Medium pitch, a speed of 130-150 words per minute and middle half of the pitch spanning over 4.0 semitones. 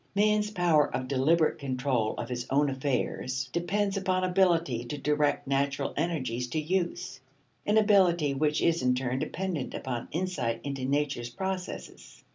Yes: medium, 150 Hz; average, 145 wpm; wide, 5.6 semitones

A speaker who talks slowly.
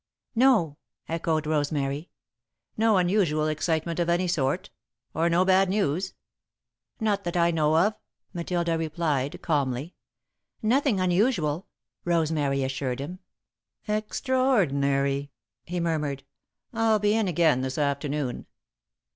Yes: slow, 110 wpm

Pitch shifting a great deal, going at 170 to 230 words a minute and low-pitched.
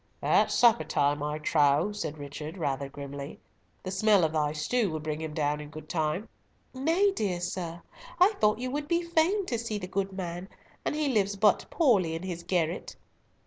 No: wide, 6.4 semitones; average, 190 wpm; medium, 180 Hz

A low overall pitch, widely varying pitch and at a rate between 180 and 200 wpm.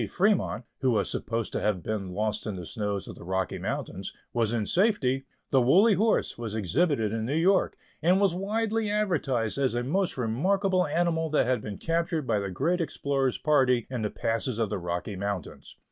Yes: low, 130 Hz; wide, 8.4 semitones; average, 190 wpm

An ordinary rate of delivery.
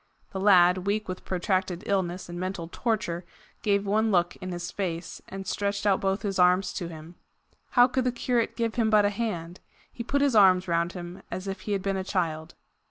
No: fast, 210 wpm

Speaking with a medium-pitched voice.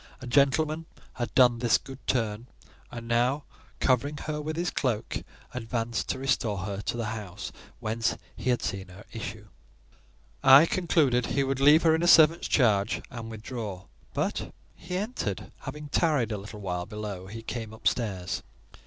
No: low, 120 Hz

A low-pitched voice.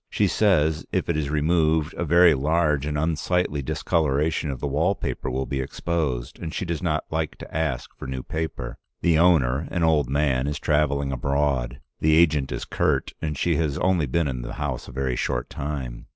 Yes: very low, 75 Hz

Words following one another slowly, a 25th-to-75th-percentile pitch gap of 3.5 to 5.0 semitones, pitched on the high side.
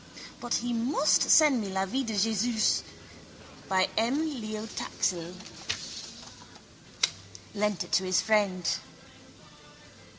Yes: slow, 105 wpm; average, 4.0 semitones; high, 215 Hz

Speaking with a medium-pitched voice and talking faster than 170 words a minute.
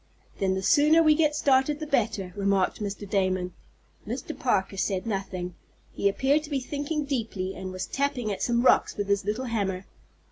No: high, 210 Hz; average, 180 wpm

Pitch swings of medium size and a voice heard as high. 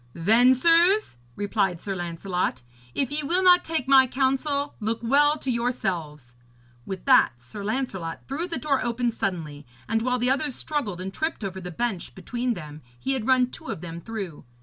No: wide, 6.8 semitones; high, 235 Hz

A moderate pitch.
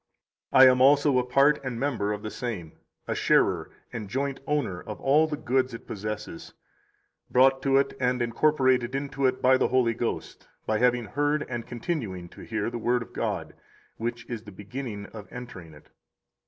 No: low, 125 Hz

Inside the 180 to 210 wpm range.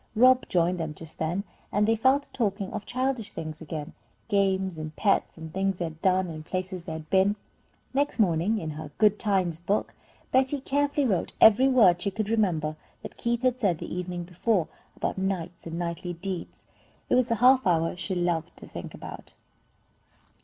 Yes: average, 190 wpm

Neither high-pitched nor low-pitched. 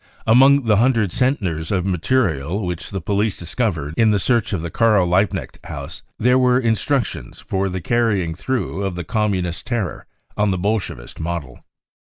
No: low, 100 Hz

